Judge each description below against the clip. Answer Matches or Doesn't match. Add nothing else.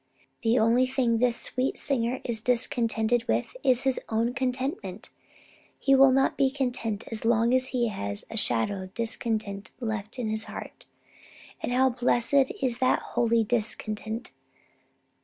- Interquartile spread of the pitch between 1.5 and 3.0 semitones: Matches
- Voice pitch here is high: Matches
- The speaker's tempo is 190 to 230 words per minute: Doesn't match